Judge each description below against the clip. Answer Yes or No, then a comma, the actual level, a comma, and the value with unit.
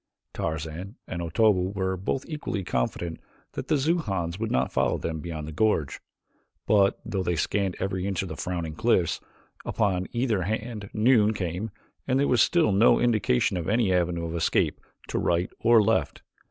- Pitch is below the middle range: Yes, very low, 95 Hz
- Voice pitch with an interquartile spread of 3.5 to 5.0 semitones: Yes, average, 4.5 semitones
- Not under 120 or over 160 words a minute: No, average, 170 wpm